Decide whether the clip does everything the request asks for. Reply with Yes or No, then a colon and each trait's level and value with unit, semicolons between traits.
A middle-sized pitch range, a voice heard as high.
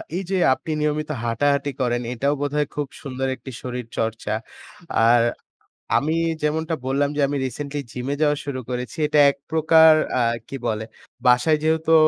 No: average, 3.4 semitones; medium, 145 Hz